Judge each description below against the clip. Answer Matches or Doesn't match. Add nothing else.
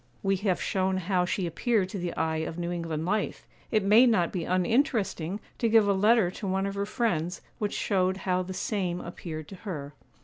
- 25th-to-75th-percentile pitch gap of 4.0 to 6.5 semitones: Doesn't match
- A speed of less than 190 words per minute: Doesn't match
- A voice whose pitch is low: Doesn't match